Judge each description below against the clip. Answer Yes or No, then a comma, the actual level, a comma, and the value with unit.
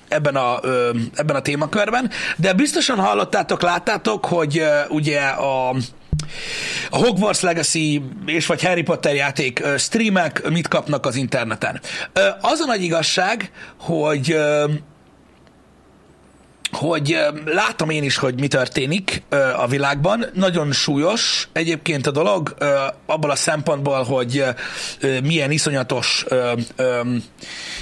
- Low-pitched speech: No, medium, 150 Hz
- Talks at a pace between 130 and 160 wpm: No, average, 110 wpm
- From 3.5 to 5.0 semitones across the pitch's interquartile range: Yes, average, 4.4 semitones